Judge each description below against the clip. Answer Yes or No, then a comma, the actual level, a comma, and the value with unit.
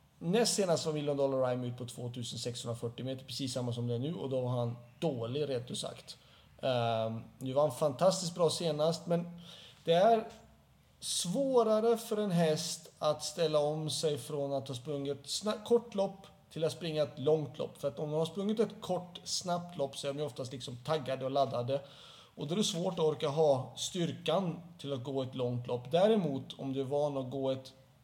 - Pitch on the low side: No, medium, 150 Hz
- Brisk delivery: Yes, fast, 210 wpm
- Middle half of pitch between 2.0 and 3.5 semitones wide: No, average, 4.3 semitones